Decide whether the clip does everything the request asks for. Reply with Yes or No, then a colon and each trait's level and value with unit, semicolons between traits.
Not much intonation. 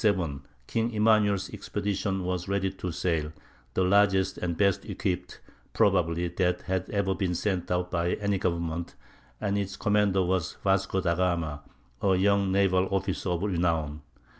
Yes: narrow, 2.3 semitones